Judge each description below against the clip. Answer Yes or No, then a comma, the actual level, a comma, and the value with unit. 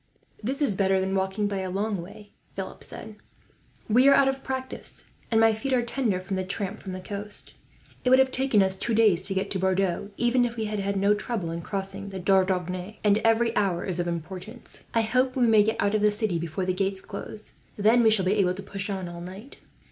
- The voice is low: No, high, 200 Hz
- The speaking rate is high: Yes, fast, 230 wpm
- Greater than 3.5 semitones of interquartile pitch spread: No, average, 2.9 semitones